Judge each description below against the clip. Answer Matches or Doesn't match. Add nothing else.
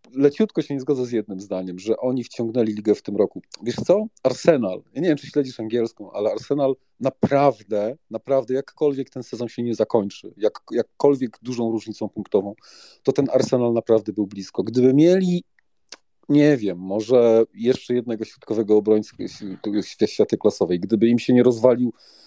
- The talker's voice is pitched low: Matches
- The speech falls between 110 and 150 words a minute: Doesn't match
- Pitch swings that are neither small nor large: Matches